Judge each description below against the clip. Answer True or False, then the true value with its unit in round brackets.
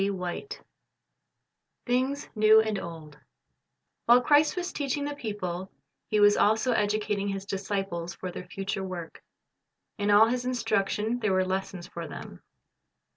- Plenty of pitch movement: False (3.9 semitones)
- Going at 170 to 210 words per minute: False (150 wpm)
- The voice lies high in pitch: True (205 Hz)